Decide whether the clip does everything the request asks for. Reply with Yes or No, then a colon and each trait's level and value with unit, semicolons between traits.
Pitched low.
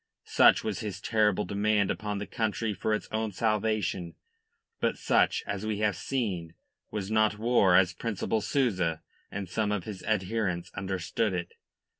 Yes: low, 105 Hz